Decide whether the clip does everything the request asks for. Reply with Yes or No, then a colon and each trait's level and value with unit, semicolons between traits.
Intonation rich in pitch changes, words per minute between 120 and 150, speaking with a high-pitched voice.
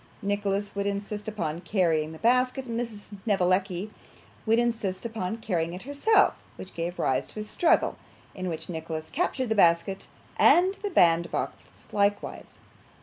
No: average, 4.6 semitones; average, 145 wpm; high, 200 Hz